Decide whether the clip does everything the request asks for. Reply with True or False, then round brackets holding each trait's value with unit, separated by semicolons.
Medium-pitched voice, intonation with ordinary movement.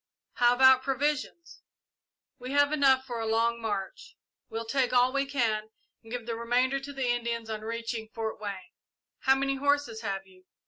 False (240 Hz; 3.1 semitones)